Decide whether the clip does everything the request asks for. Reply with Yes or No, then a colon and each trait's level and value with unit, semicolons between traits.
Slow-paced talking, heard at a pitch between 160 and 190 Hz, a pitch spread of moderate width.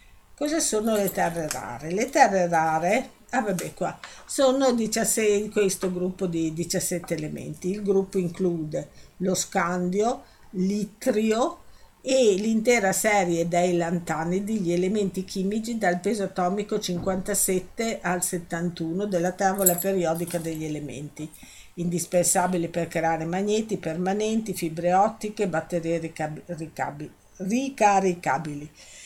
Yes: slow, 110 wpm; medium, 185 Hz; average, 3.4 semitones